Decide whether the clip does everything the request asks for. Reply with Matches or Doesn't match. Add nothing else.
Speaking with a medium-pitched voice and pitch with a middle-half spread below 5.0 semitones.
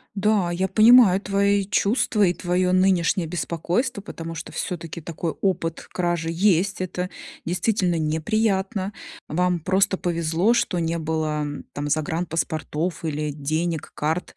Matches